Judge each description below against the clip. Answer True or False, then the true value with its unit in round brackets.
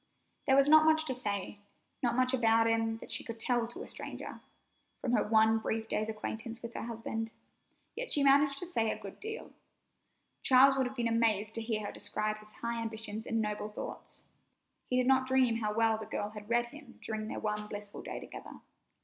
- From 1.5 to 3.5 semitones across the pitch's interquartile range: True (2.8 semitones)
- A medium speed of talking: False (210 wpm)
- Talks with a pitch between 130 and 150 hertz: False (225 Hz)